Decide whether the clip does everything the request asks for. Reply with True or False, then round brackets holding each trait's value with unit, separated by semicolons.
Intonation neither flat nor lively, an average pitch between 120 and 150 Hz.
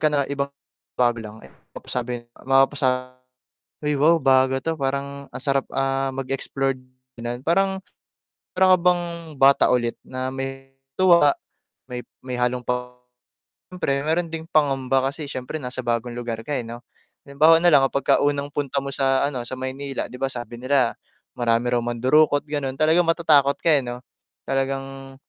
False (2.3 semitones; 135 Hz)